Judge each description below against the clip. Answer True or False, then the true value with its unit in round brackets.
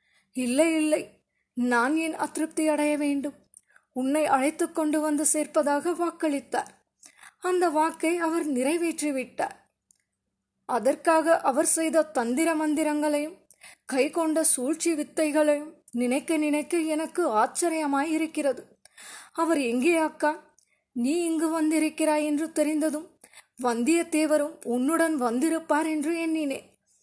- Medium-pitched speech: False (310 Hz)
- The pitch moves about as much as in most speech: False (1.8 semitones)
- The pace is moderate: True (95 wpm)